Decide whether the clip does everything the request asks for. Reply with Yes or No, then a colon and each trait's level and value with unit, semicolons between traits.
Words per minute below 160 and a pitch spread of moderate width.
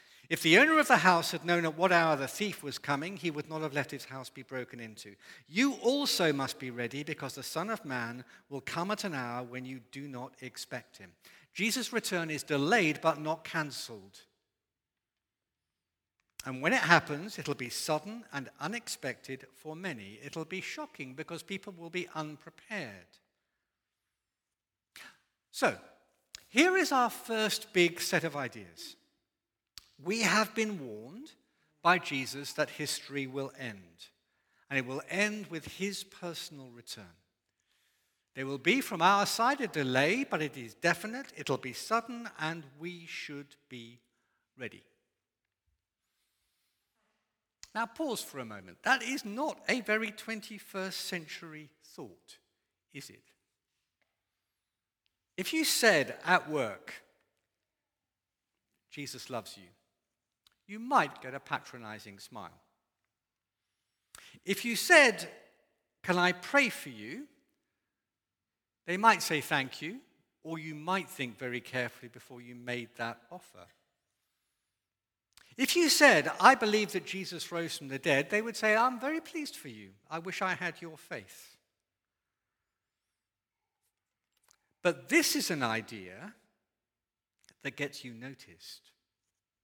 No: average, 140 wpm; wide, 8.0 semitones